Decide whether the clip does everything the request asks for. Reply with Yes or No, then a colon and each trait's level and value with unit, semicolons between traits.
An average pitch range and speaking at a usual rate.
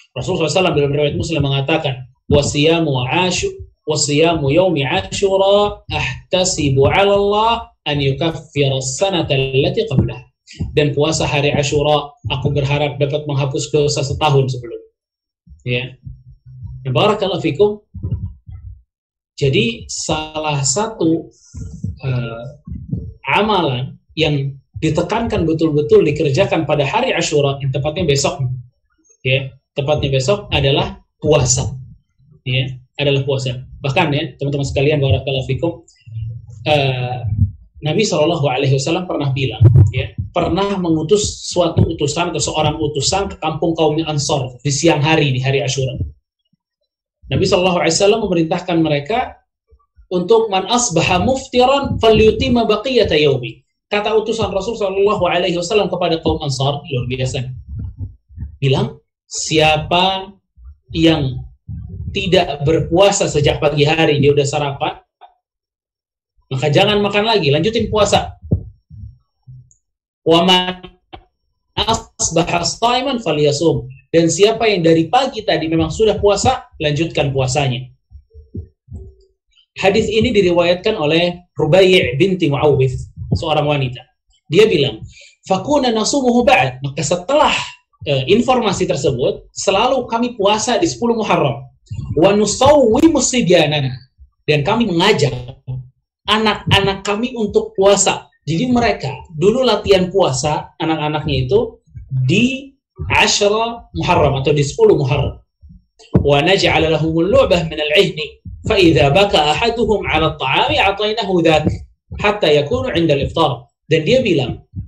No: wide, 6.2 semitones; average, 100 wpm